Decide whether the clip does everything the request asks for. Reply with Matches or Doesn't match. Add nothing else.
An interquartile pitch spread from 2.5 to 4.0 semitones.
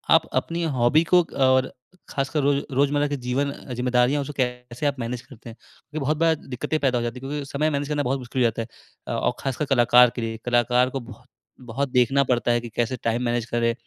Matches